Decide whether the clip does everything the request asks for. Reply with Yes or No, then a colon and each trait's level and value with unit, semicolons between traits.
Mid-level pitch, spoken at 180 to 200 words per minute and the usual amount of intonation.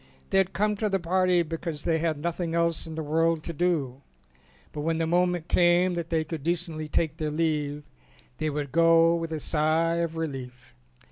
No: medium, 165 Hz; average, 195 wpm; narrow, 1.8 semitones